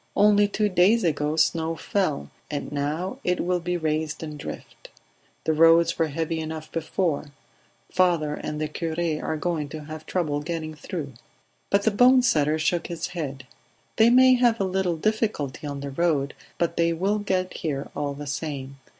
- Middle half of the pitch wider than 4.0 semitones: No, average, 3.4 semitones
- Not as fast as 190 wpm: Yes, average, 175 wpm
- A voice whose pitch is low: No, medium, 165 Hz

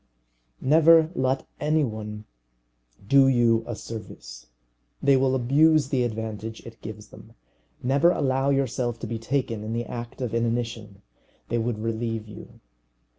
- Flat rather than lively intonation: No, average, 3.1 semitones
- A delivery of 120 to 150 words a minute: Yes, average, 140 wpm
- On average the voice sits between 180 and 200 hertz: No, low, 120 Hz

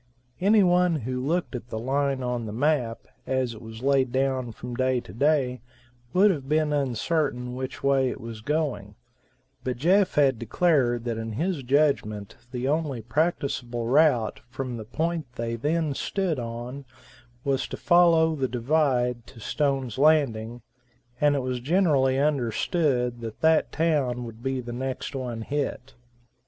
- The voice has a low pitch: Yes, low, 130 Hz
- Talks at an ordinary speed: Yes, average, 155 wpm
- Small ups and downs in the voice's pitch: No, average, 4.0 semitones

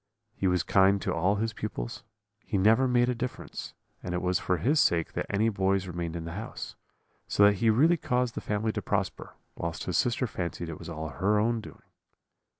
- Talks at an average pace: No, fast, 210 wpm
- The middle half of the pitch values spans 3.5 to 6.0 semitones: Yes, average, 4.5 semitones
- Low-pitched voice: Yes, low, 100 Hz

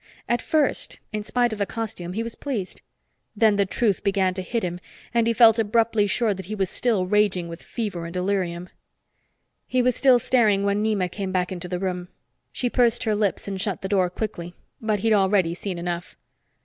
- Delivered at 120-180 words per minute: No, average, 200 wpm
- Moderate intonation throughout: Yes, average, 3.5 semitones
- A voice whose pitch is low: No, high, 200 Hz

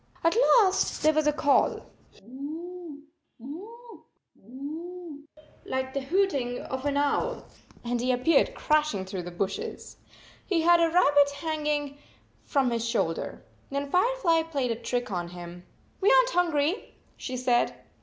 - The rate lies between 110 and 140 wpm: No, average, 155 wpm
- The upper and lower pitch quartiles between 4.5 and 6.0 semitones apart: Yes, average, 5.3 semitones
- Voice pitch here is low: No, very high, 290 Hz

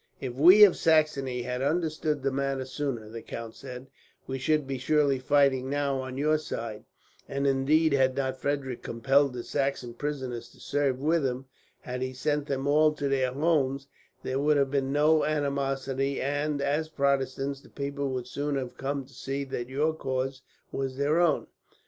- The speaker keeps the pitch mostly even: Yes, narrow, 1.9 semitones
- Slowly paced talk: No, average, 180 wpm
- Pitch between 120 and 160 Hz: Yes, medium, 140 Hz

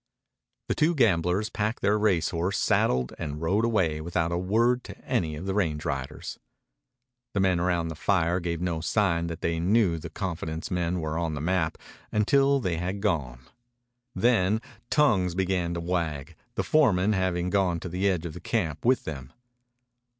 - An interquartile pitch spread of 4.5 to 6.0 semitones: No, average, 3.5 semitones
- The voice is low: Yes, very low, 90 Hz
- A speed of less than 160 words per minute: No, average, 180 wpm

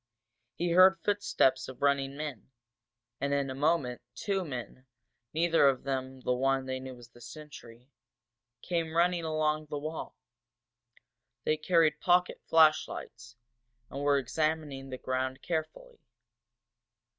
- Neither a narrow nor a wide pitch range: Yes, average, 3.7 semitones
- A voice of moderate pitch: Yes, medium, 145 Hz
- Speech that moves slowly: Yes, slow, 130 wpm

